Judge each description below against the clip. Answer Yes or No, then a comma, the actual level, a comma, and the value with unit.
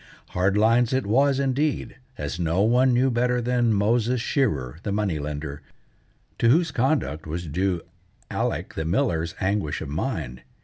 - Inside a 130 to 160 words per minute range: Yes, average, 150 wpm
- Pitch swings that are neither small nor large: No, wide, 7.4 semitones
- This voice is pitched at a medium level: No, low, 105 Hz